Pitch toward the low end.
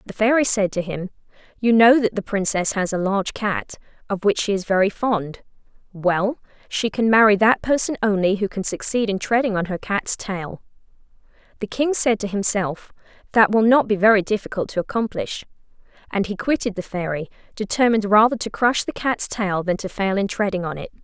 No: high, 205 Hz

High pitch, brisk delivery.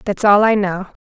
Yes: high, 200 Hz; fast, 235 wpm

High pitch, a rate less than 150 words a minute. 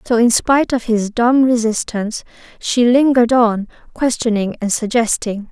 Yes: high, 230 Hz; average, 140 wpm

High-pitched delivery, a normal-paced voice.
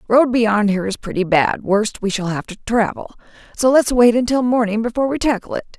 No: high, 225 Hz; fast, 220 wpm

